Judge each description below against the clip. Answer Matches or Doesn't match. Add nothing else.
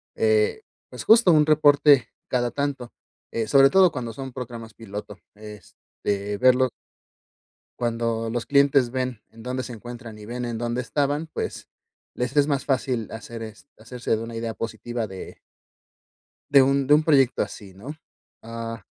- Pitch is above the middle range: Doesn't match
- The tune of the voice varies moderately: Matches